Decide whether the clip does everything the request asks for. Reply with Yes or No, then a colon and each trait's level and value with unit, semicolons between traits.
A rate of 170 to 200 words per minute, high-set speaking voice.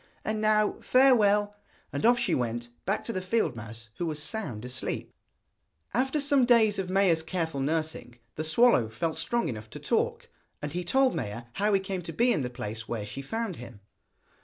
No: average, 190 wpm; medium, 175 Hz